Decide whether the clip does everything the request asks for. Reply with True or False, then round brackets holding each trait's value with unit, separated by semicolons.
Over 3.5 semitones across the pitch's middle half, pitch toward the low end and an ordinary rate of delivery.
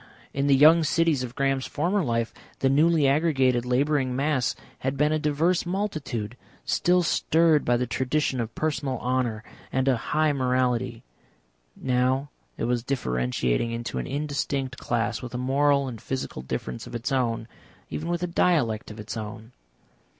True (3.9 semitones; 130 Hz; 160 wpm)